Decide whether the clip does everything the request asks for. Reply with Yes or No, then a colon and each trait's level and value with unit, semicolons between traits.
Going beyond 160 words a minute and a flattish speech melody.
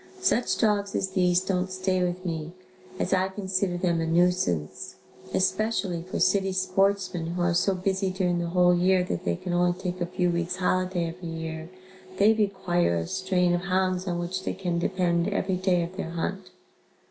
Yes: average, 185 wpm; narrow, 1.5 semitones